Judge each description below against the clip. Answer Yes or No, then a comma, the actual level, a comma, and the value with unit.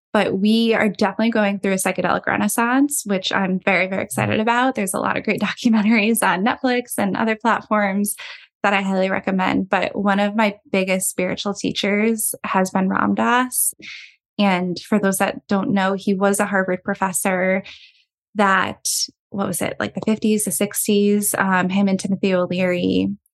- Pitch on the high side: Yes, high, 200 Hz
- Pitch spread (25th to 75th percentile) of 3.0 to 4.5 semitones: No, narrow, 2.4 semitones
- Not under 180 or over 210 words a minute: No, average, 170 wpm